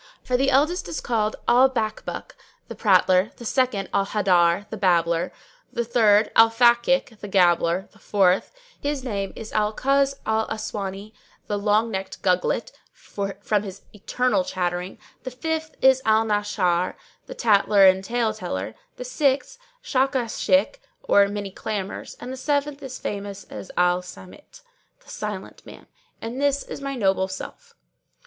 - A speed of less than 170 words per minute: Yes, average, 150 wpm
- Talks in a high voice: Yes, high, 215 Hz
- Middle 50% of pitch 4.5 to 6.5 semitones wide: Yes, average, 4.9 semitones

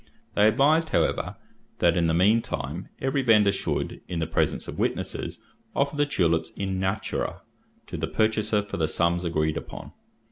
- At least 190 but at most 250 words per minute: No, average, 170 wpm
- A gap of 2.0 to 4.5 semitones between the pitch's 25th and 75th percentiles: No, average, 5.0 semitones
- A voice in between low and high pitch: No, low, 100 Hz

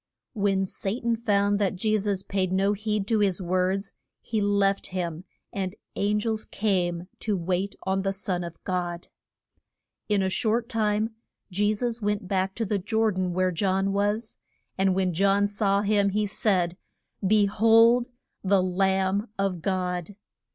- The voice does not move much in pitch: Yes, narrow, 2.0 semitones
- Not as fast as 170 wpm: Yes, average, 160 wpm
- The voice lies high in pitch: Yes, high, 195 Hz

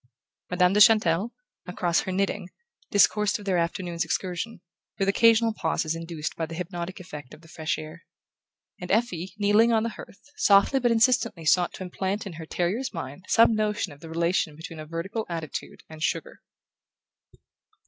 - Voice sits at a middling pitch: Yes, medium, 180 Hz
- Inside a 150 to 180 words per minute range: Yes, average, 170 wpm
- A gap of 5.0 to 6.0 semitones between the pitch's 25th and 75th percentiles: No, average, 4.0 semitones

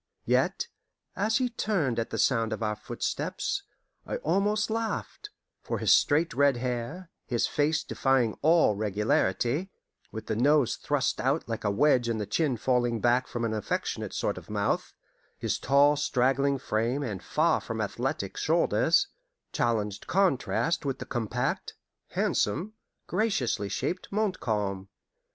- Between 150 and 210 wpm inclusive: No, average, 140 wpm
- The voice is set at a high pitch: No, low, 130 Hz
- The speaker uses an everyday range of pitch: No, wide, 6.3 semitones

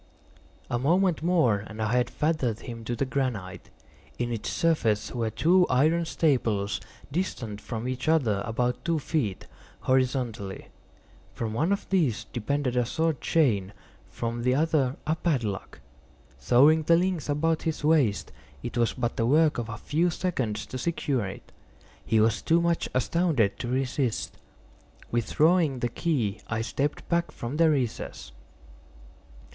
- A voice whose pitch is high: No, low, 130 Hz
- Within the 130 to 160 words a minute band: Yes, average, 150 wpm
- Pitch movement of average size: No, wide, 5.8 semitones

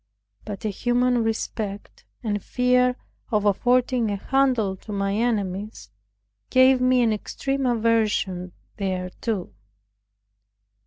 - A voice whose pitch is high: Yes, high, 225 Hz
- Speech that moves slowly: Yes, slow, 105 wpm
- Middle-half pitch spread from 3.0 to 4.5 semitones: Yes, average, 3.9 semitones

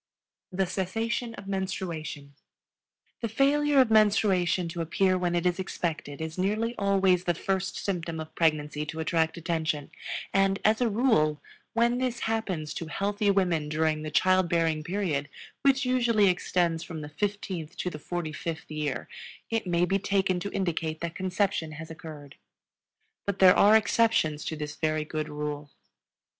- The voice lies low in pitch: No, medium, 180 Hz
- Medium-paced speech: Yes, average, 160 wpm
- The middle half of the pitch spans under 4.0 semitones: No, average, 4.3 semitones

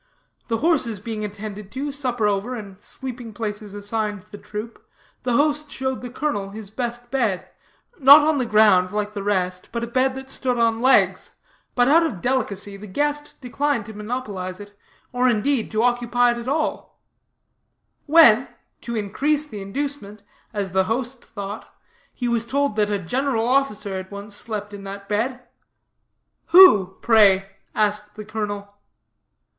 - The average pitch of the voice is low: No, high, 225 Hz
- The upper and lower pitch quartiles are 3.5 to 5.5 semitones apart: Yes, average, 4.1 semitones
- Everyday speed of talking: Yes, average, 160 wpm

